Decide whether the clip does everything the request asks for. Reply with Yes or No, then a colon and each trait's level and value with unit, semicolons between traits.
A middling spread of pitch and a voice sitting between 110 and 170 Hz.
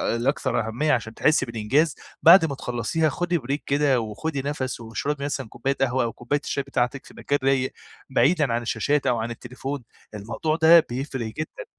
Yes: average, 3.7 semitones; low, 135 Hz